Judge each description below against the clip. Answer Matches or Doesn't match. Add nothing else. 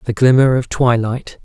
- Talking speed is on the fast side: Doesn't match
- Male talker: Matches